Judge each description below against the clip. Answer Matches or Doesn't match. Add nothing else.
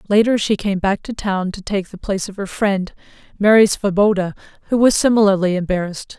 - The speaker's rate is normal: Matches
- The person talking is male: Doesn't match